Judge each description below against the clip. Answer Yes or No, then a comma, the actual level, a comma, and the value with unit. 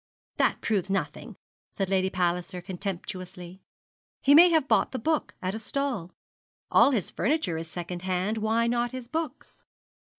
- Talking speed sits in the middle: Yes, average, 155 wpm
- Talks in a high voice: Yes, high, 195 Hz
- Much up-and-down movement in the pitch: Yes, wide, 5.9 semitones